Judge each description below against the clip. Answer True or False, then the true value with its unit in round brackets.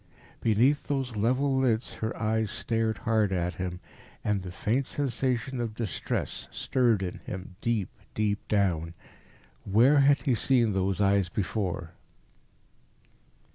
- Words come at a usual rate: False (130 wpm)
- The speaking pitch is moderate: False (110 Hz)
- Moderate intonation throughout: True (4.4 semitones)